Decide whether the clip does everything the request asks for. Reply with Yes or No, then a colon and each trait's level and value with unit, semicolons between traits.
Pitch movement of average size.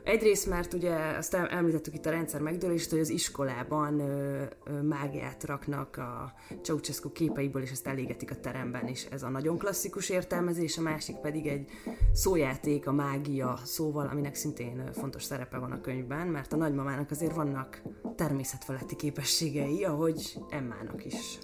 Yes: average, 3.1 semitones